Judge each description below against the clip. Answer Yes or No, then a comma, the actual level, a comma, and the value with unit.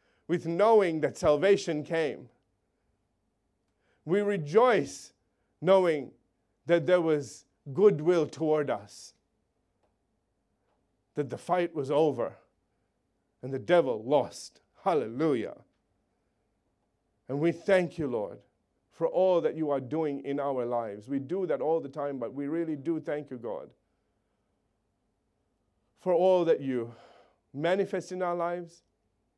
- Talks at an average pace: No, slow, 120 wpm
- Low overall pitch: No, medium, 155 Hz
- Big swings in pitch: No, average, 4.6 semitones